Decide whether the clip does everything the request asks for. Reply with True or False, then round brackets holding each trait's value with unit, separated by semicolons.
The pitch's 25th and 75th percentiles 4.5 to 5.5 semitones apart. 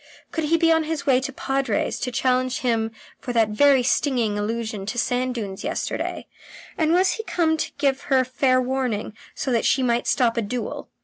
False (3.4 semitones)